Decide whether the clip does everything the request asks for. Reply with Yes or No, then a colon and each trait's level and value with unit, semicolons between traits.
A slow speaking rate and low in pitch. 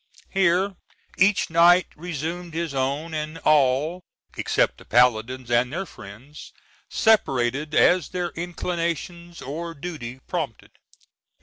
No: slow, 110 wpm; medium, 160 Hz